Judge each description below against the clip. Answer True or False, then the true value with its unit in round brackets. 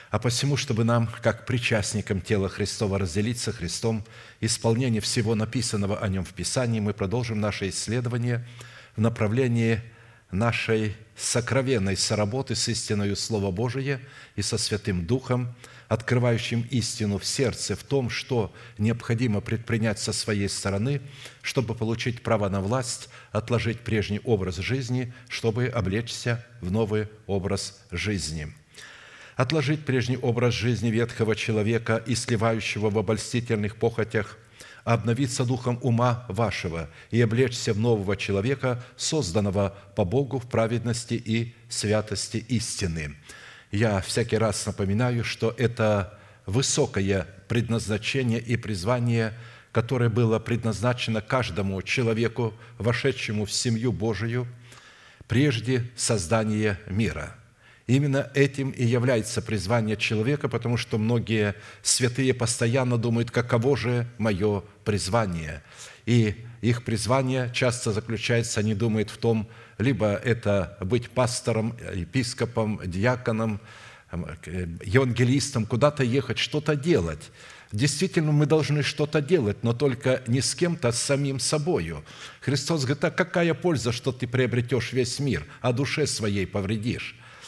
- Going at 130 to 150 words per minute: False (120 wpm)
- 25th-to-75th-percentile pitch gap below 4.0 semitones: True (2.7 semitones)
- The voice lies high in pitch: False (115 Hz)